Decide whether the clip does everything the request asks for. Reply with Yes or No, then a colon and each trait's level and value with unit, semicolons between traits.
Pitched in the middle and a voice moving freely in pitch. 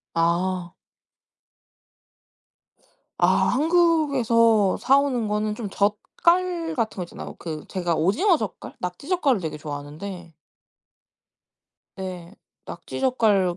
No: high, 210 Hz; wide, 7.4 semitones